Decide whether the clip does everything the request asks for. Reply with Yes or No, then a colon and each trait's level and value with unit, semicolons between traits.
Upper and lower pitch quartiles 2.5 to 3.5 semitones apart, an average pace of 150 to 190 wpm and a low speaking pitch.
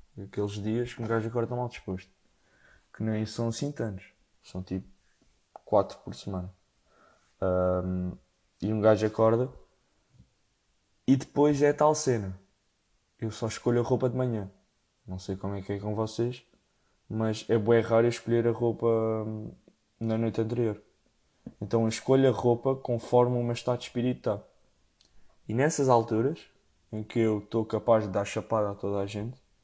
Yes: average, 3.0 semitones; average, 160 wpm; low, 110 Hz